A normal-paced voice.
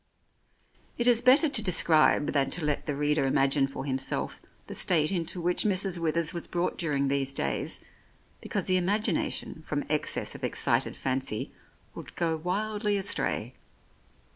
Yes: average, 155 wpm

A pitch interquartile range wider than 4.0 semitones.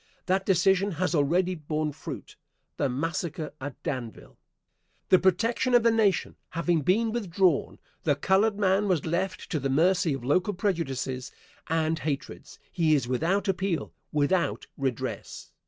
Yes: average, 4.5 semitones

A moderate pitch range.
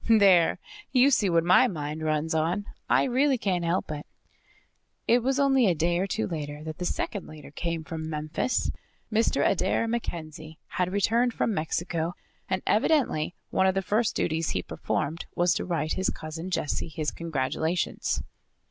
Yes: average, 4.8 semitones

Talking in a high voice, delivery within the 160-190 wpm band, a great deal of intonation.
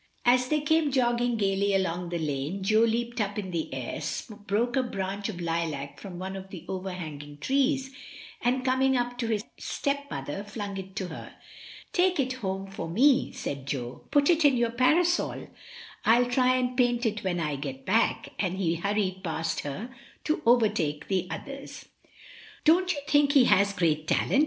Yes: high, 205 Hz; average, 175 wpm; wide, 6.2 semitones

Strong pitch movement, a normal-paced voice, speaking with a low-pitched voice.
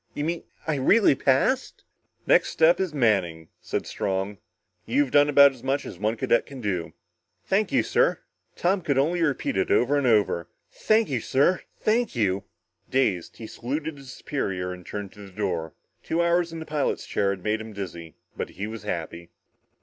Yes: wide, 7.7 semitones; average, 180 wpm; low, 130 Hz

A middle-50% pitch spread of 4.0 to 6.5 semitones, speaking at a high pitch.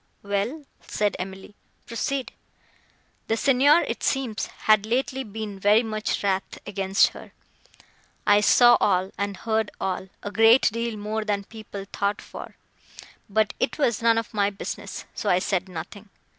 No: narrow, 2.4 semitones; high, 210 Hz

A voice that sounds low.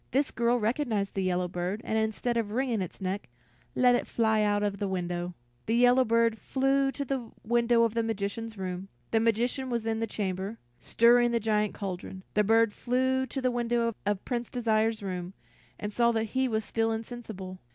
No: high, 225 Hz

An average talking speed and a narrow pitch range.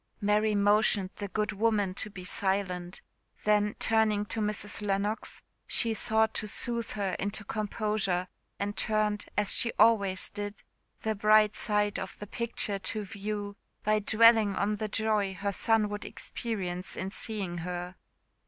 Yes: average, 150 wpm; narrow, 1.4 semitones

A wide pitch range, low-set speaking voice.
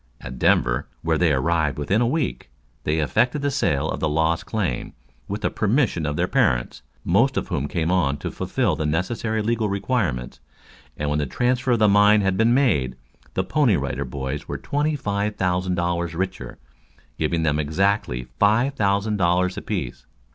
Yes: wide, 6.4 semitones; very low, 90 Hz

